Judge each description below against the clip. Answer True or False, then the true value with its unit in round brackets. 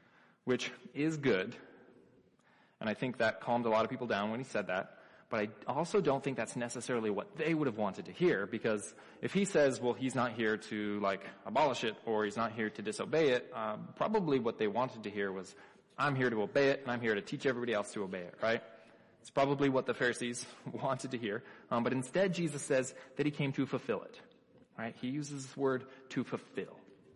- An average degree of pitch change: True (3.5 semitones)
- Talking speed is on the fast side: True (220 wpm)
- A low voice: True (125 Hz)